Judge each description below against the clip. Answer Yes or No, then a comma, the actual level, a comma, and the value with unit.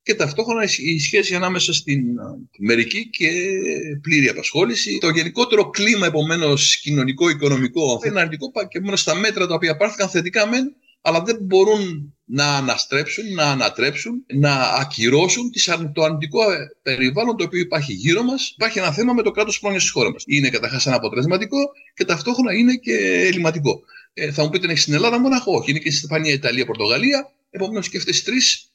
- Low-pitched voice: No, medium, 175 Hz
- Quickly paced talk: Yes, fast, 180 wpm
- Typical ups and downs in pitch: No, wide, 6.5 semitones